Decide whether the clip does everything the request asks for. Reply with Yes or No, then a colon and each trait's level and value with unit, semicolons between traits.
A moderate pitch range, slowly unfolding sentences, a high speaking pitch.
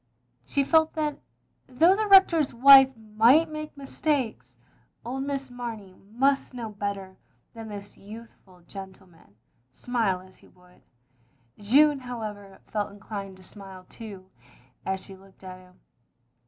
No: wide, 6.0 semitones; slow, 130 wpm; high, 220 Hz